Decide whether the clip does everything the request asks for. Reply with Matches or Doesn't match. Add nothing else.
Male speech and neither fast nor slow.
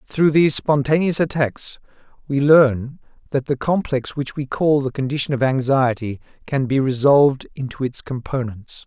Matches